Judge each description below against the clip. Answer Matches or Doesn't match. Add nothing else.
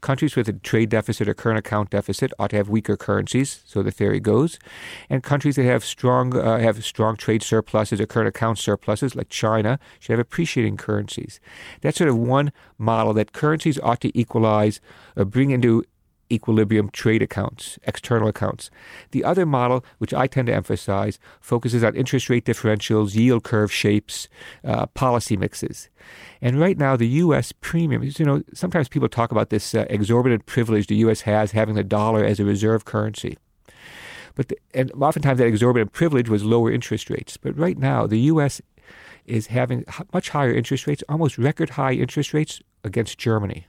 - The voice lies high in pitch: Doesn't match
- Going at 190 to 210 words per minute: Doesn't match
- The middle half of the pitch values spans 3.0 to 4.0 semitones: Matches